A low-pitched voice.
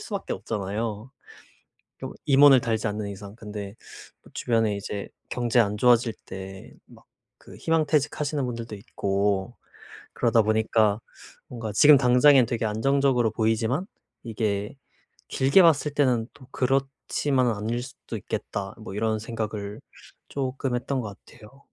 Yes: low, 115 Hz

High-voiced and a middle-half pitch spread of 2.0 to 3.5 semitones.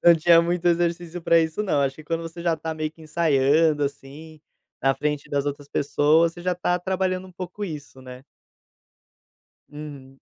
No: medium, 160 Hz; average, 3.0 semitones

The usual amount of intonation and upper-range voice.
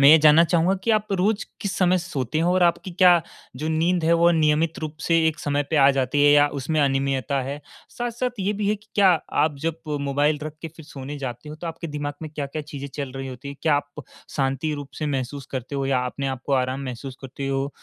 No: average, 3.4 semitones; medium, 150 Hz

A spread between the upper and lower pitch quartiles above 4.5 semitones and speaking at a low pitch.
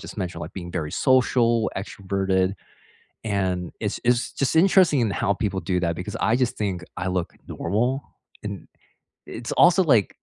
Yes: average, 4.9 semitones; low, 100 Hz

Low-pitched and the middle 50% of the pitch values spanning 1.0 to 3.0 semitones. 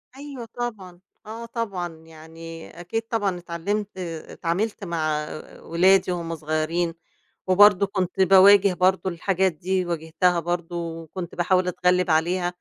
No: medium, 180 Hz; narrow, 2.6 semitones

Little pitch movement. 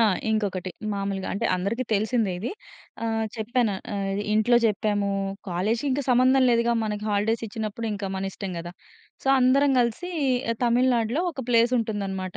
No: average, 3.2 semitones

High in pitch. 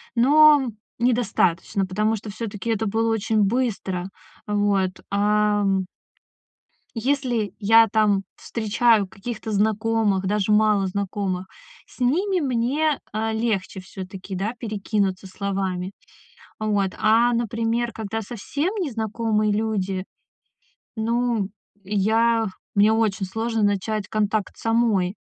Yes: high, 215 Hz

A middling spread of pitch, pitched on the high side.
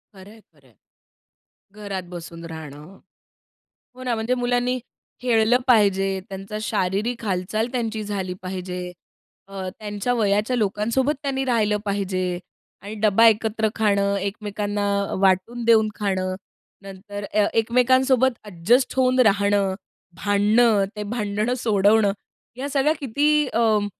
Yes: average, 3.3 semitones; high, 210 Hz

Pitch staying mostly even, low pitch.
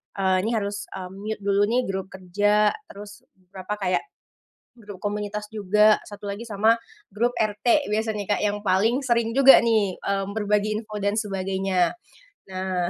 No: narrow, 1.8 semitones; high, 205 Hz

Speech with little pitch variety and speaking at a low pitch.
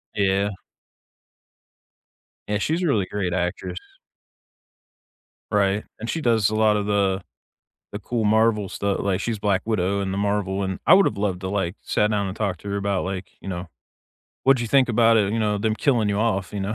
Yes: narrow, 2.1 semitones; low, 100 Hz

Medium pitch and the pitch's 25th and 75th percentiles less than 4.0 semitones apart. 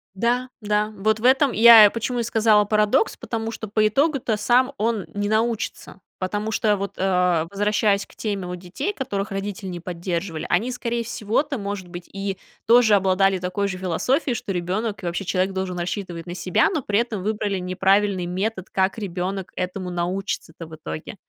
No: high, 200 Hz; average, 3.3 semitones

